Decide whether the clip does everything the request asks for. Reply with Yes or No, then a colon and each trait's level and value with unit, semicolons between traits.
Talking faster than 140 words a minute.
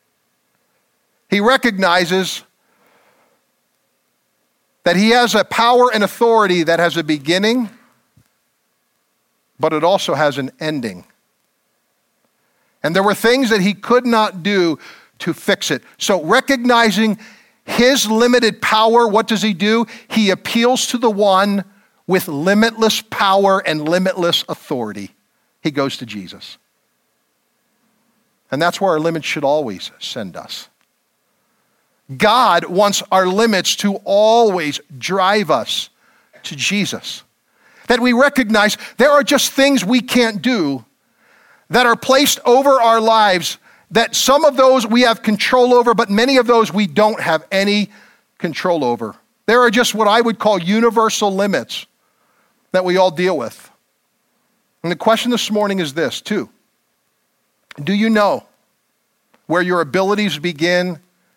No: slow, 135 wpm